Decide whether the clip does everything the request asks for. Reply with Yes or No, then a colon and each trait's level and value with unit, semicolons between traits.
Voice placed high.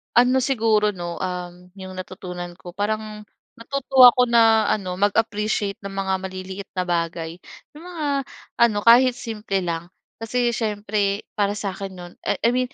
Yes: high, 205 Hz